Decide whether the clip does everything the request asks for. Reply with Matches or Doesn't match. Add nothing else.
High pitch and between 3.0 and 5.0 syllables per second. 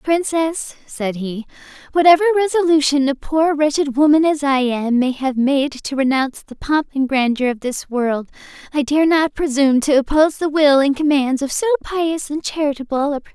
Doesn't match